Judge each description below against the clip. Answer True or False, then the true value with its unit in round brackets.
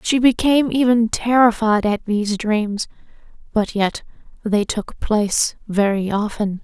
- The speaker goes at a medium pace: False (125 wpm)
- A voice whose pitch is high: True (220 Hz)